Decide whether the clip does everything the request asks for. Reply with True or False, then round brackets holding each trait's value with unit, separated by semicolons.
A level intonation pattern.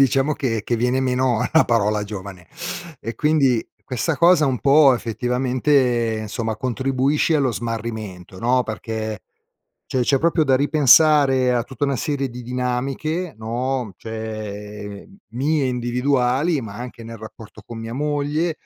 False (3.6 semitones)